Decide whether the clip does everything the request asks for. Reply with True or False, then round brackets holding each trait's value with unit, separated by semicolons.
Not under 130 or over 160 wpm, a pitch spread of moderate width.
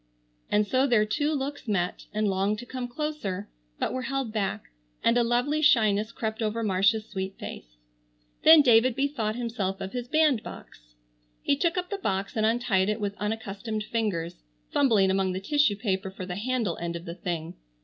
False (180 wpm; 4.6 semitones)